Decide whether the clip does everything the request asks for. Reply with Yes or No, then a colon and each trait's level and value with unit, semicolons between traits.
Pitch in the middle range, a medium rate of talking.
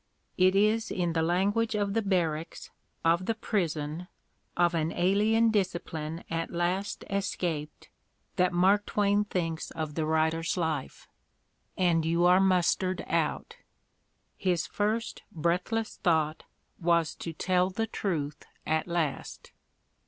No: medium, 175 Hz; slow, 125 wpm